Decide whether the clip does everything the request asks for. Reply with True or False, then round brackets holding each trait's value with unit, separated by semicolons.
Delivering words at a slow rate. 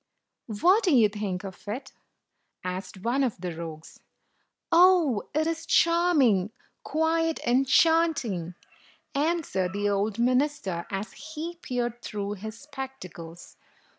True (120 wpm)